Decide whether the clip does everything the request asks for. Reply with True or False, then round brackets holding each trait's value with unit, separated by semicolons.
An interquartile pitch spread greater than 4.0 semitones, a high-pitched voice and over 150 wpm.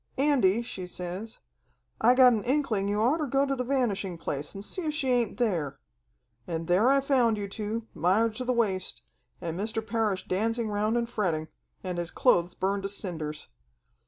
True (4.9 semitones; 215 Hz; 185 wpm)